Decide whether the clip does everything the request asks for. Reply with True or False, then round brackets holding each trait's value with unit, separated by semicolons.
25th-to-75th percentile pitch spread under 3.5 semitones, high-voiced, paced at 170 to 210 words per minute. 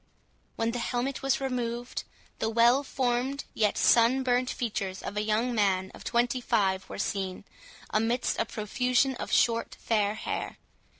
False (2.9 semitones; 235 Hz; 155 wpm)